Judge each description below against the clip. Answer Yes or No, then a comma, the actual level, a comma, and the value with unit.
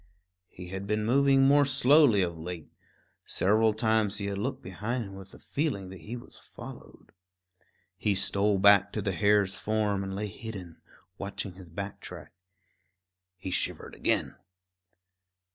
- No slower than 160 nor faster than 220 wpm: No, average, 150 wpm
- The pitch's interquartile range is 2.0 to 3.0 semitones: Yes, average, 2.7 semitones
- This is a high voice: No, low, 100 Hz